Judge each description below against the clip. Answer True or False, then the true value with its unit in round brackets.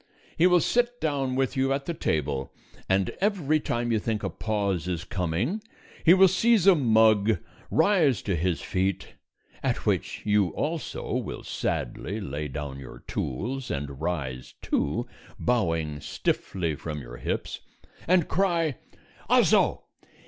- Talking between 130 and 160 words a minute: True (140 wpm)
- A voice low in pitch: True (110 Hz)